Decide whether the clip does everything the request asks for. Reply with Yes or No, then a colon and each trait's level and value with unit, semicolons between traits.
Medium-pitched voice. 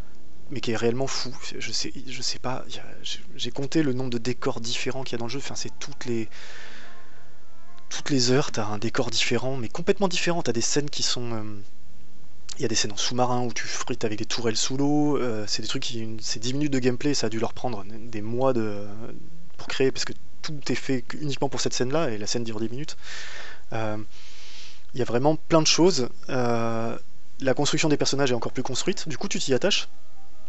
No: low, 120 Hz